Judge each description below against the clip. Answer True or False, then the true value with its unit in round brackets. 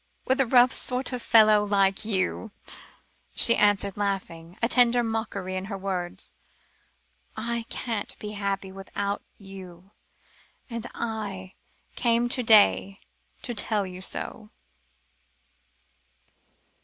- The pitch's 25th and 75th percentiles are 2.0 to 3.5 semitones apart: True (3.1 semitones)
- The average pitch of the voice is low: False (205 Hz)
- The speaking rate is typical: False (115 wpm)